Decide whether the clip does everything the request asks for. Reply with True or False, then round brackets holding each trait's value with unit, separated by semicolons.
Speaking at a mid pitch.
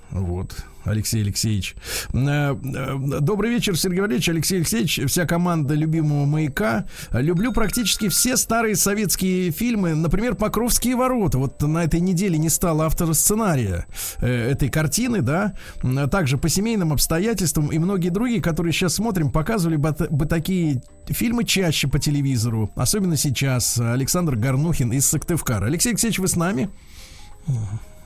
True (160 Hz)